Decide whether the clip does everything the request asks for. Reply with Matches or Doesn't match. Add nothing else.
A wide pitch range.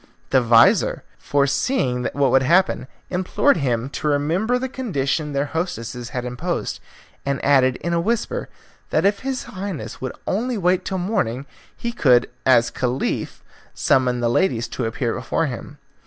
Matches